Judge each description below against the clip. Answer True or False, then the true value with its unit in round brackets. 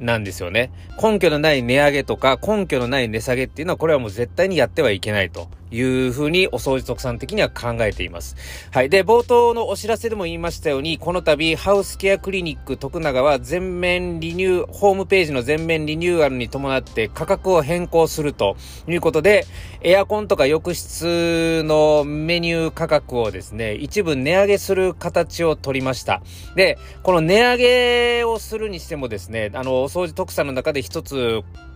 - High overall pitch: False (155 Hz)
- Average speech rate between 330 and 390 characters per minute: True (380 characters per minute)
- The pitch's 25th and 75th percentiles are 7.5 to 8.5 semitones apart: False (6.3 semitones)